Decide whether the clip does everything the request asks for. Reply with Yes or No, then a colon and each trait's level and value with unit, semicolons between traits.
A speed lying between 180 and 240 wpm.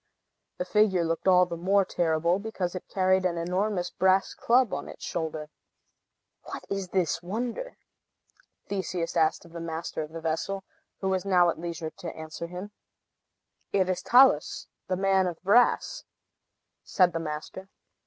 No: average, 155 wpm